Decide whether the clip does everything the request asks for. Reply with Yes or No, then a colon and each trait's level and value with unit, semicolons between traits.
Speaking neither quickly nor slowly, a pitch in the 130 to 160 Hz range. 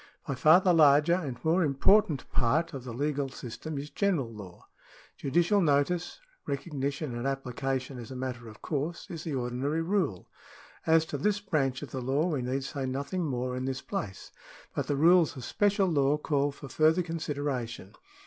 Yes: average, 185 wpm; medium, 140 Hz